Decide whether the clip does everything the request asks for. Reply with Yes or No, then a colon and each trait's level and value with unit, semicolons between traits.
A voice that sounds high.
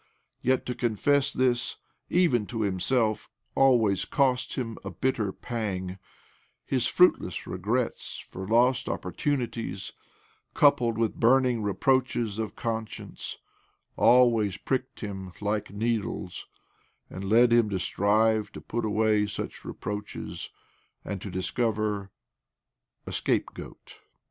No: low, 110 Hz